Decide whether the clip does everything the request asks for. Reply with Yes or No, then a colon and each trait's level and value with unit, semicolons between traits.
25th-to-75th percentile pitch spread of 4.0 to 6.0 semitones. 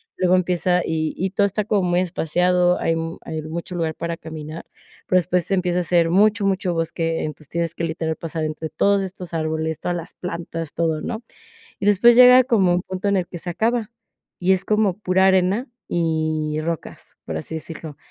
No: average, 2.8 semitones